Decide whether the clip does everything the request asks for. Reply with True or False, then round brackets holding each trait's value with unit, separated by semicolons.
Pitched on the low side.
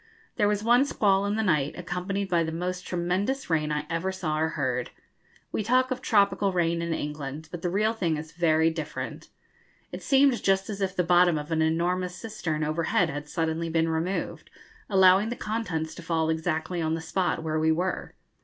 False (175 Hz)